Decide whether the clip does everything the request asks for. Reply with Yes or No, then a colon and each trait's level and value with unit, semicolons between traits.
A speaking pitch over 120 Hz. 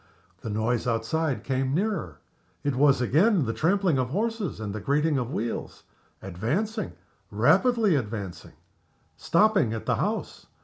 Yes: medium, 140 Hz